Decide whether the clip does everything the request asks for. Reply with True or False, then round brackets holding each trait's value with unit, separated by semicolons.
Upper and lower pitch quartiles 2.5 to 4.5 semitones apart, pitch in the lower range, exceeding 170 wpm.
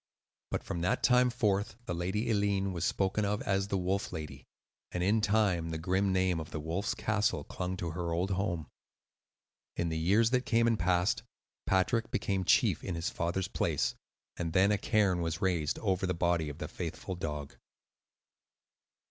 True (3.2 semitones; 95 Hz; 180 wpm)